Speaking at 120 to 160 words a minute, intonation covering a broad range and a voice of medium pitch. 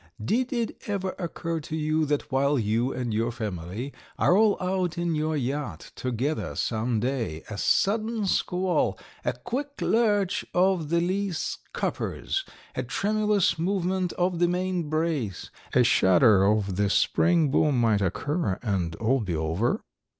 Yes: average, 150 wpm; wide, 8.2 semitones; medium, 155 Hz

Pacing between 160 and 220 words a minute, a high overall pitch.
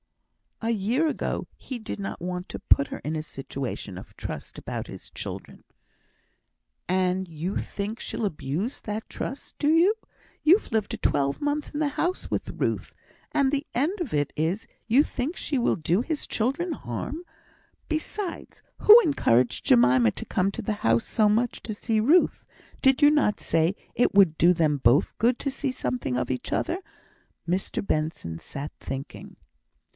Yes: average, 170 wpm; high, 210 Hz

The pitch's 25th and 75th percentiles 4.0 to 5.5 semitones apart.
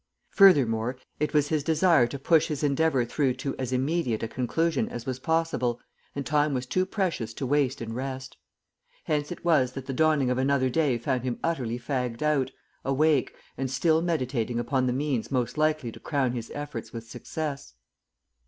No: average, 3.5 semitones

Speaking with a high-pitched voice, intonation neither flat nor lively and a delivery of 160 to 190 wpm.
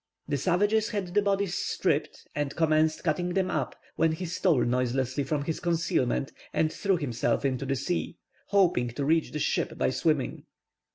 No: medium, 160 Hz; average, 4.7 semitones; average, 170 wpm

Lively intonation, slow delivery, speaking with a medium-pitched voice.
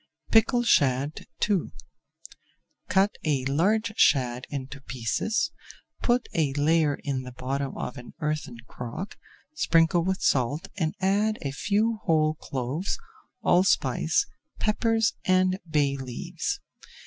Yes: wide, 6.6 semitones; slow, 115 wpm; medium, 155 Hz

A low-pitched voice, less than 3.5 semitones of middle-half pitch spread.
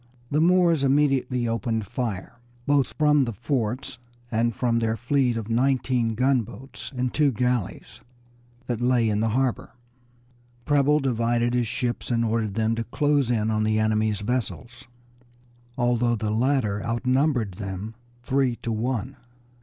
Yes: low, 120 Hz; average, 2.9 semitones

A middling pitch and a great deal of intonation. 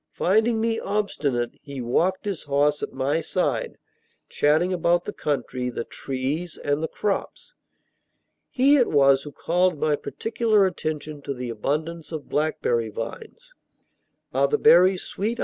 Yes: medium, 160 Hz; wide, 5.9 semitones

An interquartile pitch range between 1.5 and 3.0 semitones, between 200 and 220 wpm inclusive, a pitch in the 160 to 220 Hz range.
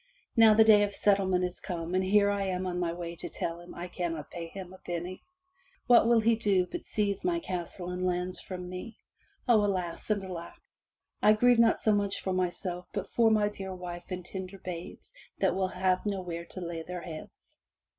Yes: narrow, 2.6 semitones; fast, 205 wpm; medium, 185 Hz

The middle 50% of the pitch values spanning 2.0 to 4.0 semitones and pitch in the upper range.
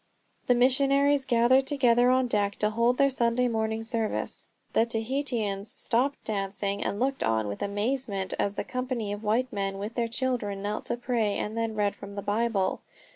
Yes: average, 3.6 semitones; high, 230 Hz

